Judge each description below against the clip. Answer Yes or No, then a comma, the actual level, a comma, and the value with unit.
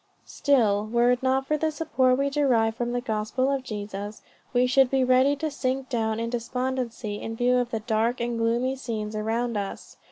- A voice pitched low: No, high, 245 Hz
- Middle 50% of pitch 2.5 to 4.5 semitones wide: Yes, average, 2.8 semitones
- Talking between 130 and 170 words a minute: No, average, 195 wpm